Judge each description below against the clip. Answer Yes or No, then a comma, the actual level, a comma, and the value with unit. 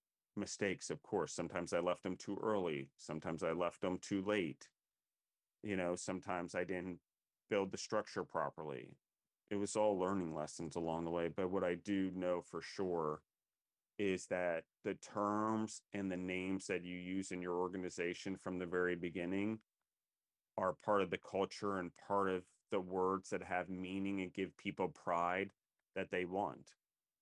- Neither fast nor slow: Yes, average, 170 wpm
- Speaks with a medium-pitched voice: No, very low, 90 Hz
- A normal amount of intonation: No, narrow, 1.7 semitones